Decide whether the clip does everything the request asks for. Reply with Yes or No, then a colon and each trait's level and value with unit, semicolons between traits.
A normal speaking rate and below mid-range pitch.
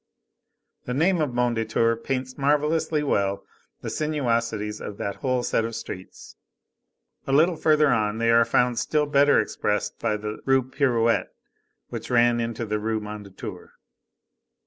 Yes: average, 145 wpm; low, 120 Hz